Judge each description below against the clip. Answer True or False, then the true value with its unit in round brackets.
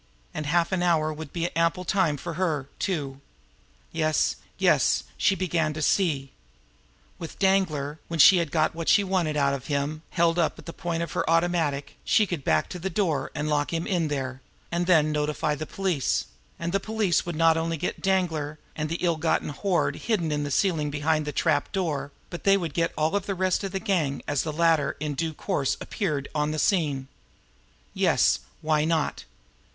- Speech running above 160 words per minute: True (195 wpm)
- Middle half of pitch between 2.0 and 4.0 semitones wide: True (3.0 semitones)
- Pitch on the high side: False (160 Hz)